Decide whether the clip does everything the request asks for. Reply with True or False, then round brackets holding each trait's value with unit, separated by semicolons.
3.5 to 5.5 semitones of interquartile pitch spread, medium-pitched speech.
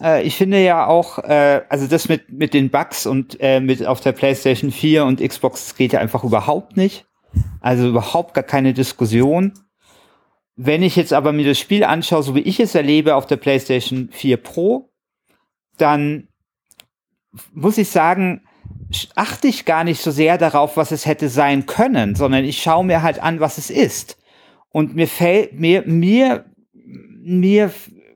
True (4.1 semitones; 155 Hz)